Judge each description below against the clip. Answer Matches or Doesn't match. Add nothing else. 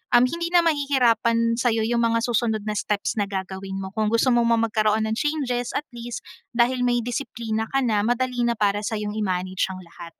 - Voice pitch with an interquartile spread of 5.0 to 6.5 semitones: Doesn't match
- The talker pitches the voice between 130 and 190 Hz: Doesn't match